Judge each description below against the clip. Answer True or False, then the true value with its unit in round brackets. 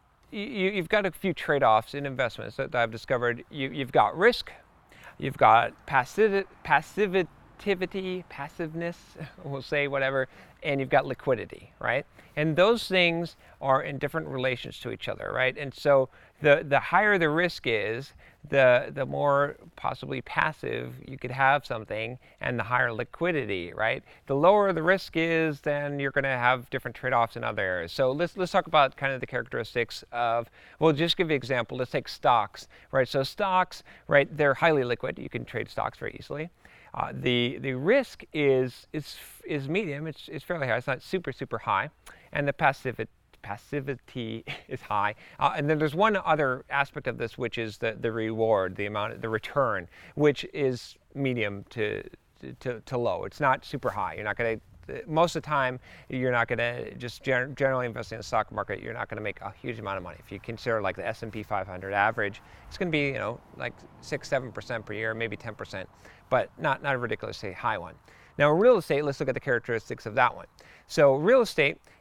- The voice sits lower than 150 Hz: True (135 Hz)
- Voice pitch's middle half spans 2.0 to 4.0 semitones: False (5.0 semitones)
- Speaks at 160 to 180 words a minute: False (190 wpm)